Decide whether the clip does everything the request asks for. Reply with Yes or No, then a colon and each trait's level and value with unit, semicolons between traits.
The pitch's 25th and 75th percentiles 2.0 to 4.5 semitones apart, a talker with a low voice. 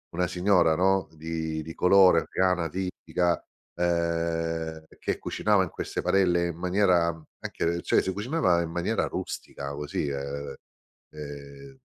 Yes: narrow, 2.5 semitones; very low, 85 Hz